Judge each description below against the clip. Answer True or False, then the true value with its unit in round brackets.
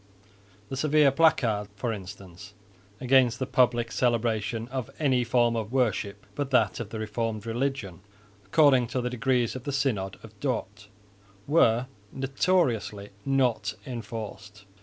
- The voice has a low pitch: True (120 Hz)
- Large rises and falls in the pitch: False (3.8 semitones)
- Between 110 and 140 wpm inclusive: True (135 wpm)